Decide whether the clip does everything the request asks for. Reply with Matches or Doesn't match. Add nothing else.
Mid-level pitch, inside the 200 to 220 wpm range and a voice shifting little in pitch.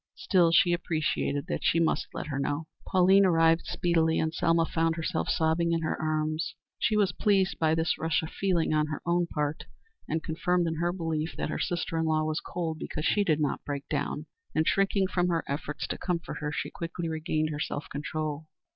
Matches